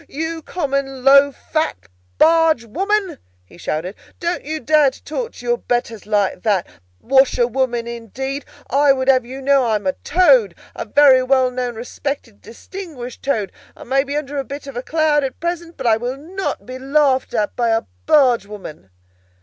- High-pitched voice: Yes, very high, 270 Hz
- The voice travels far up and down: No, average, 3.9 semitones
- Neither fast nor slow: Yes, average, 180 wpm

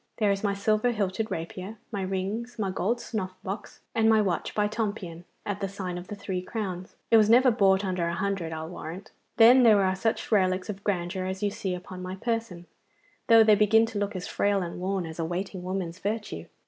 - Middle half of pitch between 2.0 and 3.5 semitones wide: Yes, average, 2.7 semitones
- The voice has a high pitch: Yes, high, 195 Hz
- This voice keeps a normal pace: No, fast, 215 wpm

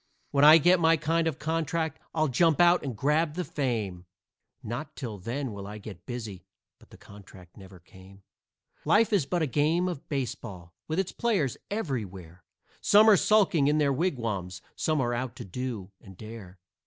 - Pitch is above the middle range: No, low, 135 Hz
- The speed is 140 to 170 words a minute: No, average, 180 wpm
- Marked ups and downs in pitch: Yes, wide, 8.1 semitones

